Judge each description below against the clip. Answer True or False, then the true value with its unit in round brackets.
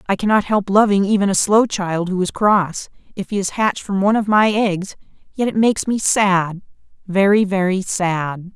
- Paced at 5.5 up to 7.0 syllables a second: False (5.0 syllables/s)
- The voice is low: False (195 Hz)